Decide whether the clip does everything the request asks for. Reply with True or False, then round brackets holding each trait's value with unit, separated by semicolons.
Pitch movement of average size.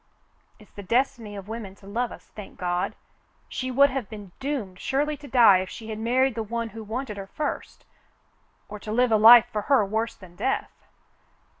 True (3.7 semitones)